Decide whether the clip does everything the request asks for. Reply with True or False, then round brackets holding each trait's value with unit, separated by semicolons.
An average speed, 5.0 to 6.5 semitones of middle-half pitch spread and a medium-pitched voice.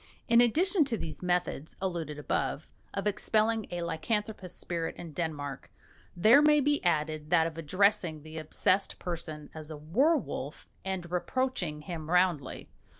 True (150 wpm; 5.4 semitones; 175 Hz)